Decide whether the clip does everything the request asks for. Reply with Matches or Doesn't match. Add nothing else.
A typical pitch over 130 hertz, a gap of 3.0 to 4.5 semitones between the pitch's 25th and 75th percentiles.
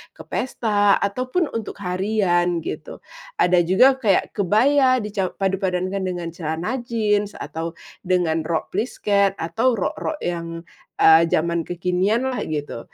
Matches